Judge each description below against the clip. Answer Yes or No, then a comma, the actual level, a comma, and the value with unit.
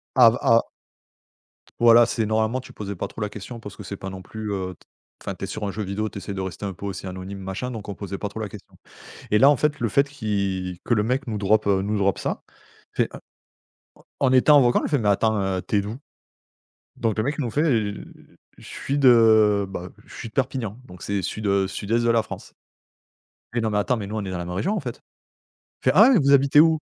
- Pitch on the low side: Yes, low, 110 Hz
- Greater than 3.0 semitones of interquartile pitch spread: Yes, average, 3.6 semitones